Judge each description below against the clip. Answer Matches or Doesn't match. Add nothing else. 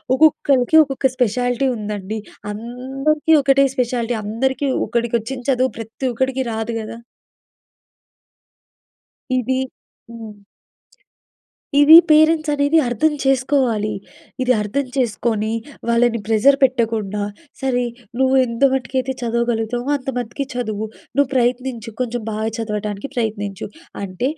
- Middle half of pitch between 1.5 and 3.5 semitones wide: Matches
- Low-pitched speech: Doesn't match